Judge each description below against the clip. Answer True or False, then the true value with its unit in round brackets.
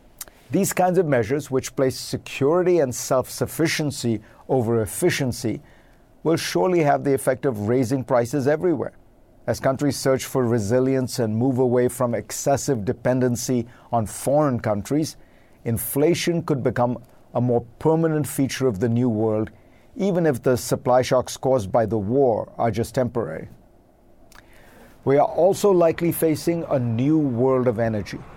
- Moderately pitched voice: False (130 Hz)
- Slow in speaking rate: False (145 wpm)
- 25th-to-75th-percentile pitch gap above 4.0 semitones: False (3.7 semitones)